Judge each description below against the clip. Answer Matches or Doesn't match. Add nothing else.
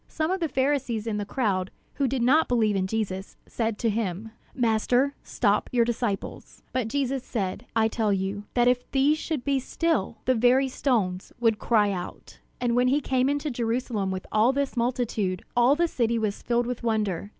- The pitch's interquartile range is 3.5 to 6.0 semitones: Matches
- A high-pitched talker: Matches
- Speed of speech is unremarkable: Matches